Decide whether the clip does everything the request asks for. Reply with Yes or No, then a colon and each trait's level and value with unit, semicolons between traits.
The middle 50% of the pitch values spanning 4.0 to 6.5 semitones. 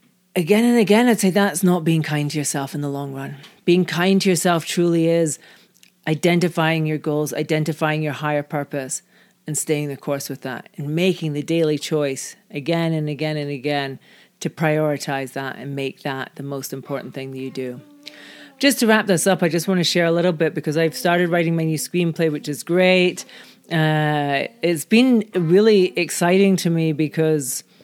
No: average, 3.5 semitones